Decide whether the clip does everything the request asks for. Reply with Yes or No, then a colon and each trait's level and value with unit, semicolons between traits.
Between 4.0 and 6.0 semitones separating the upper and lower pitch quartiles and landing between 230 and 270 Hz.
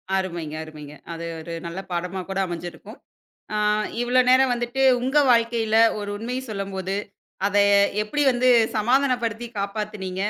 No: average, 4.6 semitones; high, 210 Hz